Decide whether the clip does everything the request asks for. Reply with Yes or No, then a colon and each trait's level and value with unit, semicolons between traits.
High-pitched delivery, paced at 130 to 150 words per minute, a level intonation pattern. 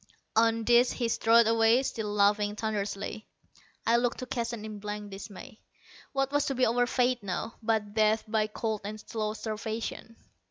No: high, 220 Hz; average, 165 wpm; narrow, 2.0 semitones